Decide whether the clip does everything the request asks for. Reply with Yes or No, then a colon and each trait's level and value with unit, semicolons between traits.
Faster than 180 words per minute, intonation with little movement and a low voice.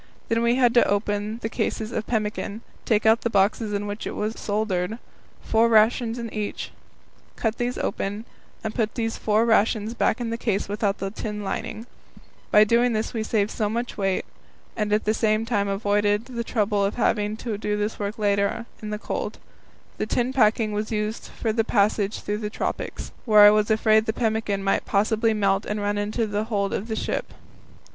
No: average, 200 wpm; narrow, 1.5 semitones; high, 215 Hz